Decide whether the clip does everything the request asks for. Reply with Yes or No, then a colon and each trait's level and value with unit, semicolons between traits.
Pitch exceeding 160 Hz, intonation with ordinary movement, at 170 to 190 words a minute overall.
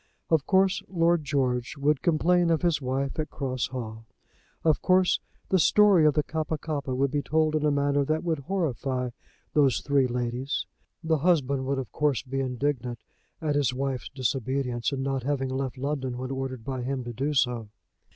No: medium, 140 Hz; average, 3.1 semitones; average, 180 wpm